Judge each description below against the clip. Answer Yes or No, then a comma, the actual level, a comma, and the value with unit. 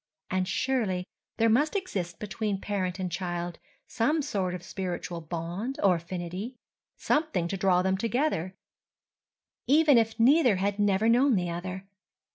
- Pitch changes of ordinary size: Yes, average, 4.6 semitones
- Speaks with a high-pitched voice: Yes, high, 195 Hz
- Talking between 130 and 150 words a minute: Yes, slow, 135 wpm